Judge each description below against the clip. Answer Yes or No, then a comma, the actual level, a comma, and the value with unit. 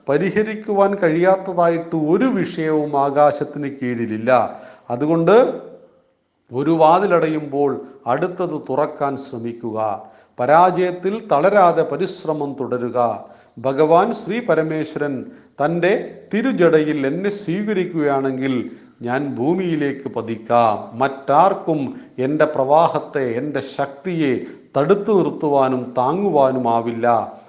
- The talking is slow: Yes, slow, 75 wpm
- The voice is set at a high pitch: No, medium, 150 Hz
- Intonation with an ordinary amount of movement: Yes, average, 4.9 semitones